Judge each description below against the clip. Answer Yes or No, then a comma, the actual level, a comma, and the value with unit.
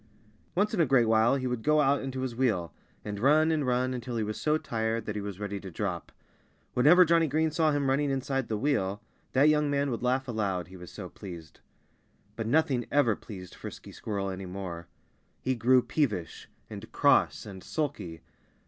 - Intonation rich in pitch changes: Yes, wide, 5.9 semitones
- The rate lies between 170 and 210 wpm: Yes, average, 195 wpm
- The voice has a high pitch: No, low, 120 Hz